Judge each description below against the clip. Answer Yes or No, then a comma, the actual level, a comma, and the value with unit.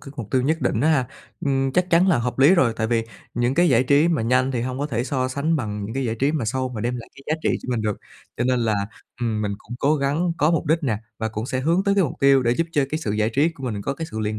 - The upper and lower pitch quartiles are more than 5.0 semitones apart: No, average, 4.7 semitones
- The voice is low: Yes, low, 130 Hz